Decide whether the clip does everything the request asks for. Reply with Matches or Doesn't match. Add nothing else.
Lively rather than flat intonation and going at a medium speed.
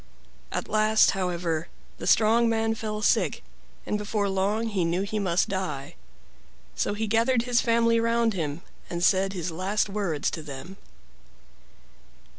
Doesn't match